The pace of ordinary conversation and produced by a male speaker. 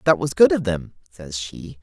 No: fast, 230 wpm; male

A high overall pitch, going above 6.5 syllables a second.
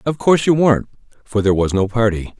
No: low, 115 Hz; 6.8 syllables/s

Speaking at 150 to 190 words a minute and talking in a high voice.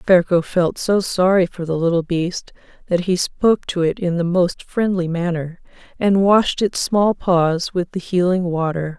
No: average, 180 wpm; medium, 180 Hz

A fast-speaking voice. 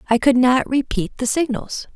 No: average, 185 wpm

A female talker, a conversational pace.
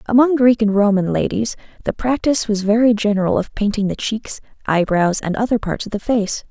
Yes: female; average, 195 wpm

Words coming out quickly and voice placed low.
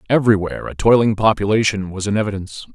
No: average, 155 wpm; low, 105 Hz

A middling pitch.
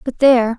No: high, 245 Hz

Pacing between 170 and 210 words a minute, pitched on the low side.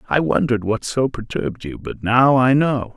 Yes: fast, 205 wpm; low, 120 Hz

